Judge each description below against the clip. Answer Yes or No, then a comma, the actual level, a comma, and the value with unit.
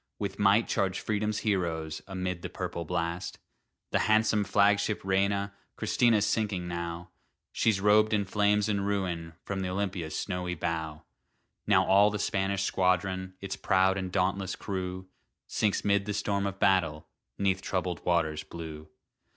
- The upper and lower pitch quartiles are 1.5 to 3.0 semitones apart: Yes, narrow, 2.4 semitones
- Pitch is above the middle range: No, very low, 95 Hz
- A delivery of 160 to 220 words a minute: No, average, 145 wpm